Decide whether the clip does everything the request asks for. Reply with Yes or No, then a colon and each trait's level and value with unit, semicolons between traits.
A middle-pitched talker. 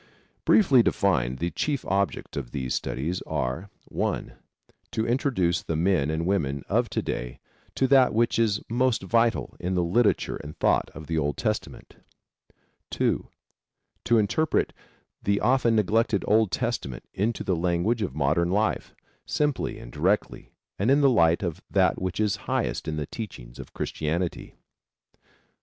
No: very low, 95 Hz